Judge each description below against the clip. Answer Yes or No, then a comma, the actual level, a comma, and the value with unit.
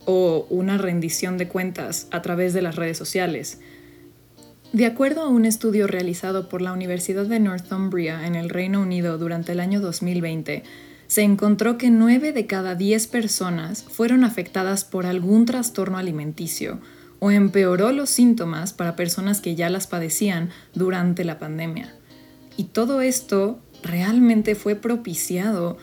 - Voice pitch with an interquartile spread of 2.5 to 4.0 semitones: Yes, average, 3.5 semitones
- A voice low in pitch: No, medium, 185 Hz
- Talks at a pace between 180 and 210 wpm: No, average, 145 wpm